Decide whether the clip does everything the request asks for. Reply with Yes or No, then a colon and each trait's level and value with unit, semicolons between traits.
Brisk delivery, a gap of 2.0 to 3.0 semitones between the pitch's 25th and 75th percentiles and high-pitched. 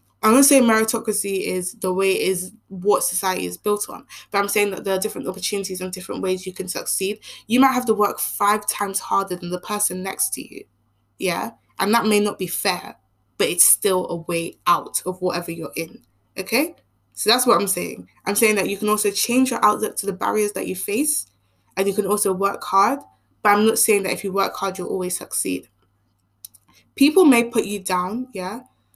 Yes: fast, 220 wpm; narrow, 2.6 semitones; high, 195 Hz